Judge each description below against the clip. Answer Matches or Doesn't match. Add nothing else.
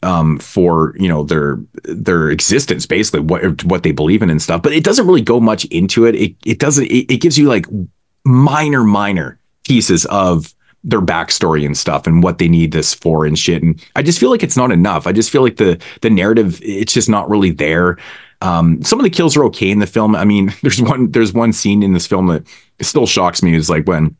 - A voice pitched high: Doesn't match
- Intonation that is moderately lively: Doesn't match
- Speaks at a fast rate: Matches